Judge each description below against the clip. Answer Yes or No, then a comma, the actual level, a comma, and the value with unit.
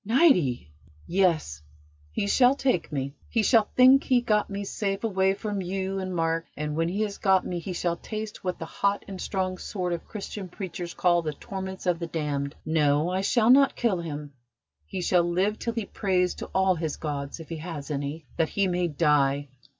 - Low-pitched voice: No, medium, 180 Hz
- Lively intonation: No, average, 3.9 semitones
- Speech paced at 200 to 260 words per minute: Yes, fast, 205 wpm